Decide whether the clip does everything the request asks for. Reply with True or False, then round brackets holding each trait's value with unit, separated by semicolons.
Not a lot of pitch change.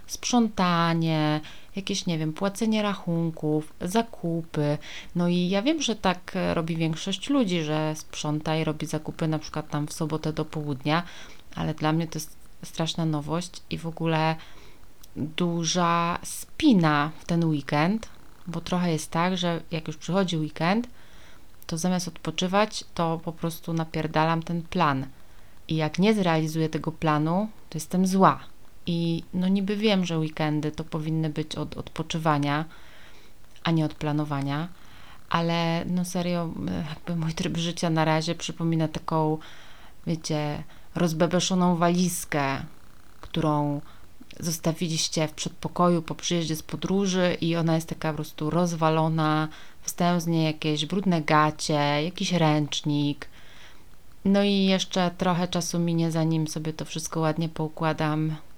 True (2.2 semitones)